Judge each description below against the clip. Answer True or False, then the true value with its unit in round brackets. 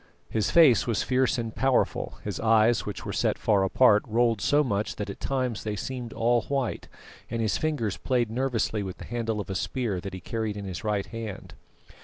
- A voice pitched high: False (115 Hz)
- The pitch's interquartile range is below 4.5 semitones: True (3.1 semitones)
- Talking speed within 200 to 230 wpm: True (205 wpm)